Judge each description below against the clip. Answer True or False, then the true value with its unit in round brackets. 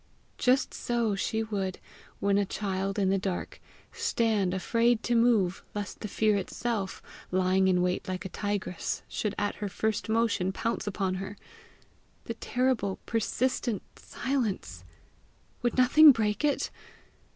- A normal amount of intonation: True (3.4 semitones)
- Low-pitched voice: False (205 Hz)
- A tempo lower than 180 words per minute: True (140 wpm)